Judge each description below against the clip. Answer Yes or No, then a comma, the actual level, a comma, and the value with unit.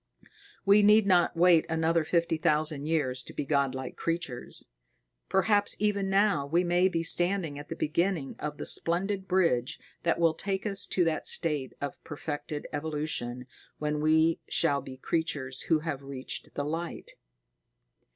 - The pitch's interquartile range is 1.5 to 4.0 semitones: Yes, average, 3.6 semitones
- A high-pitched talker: No, medium, 160 Hz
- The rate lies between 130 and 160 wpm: Yes, average, 150 wpm